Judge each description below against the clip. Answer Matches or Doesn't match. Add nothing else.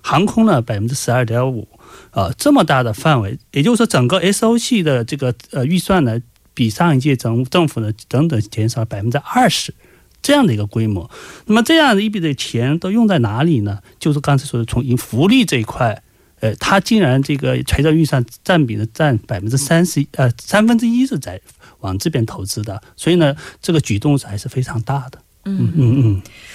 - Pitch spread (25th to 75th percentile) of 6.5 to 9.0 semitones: Matches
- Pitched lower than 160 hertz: Matches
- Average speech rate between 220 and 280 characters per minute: Doesn't match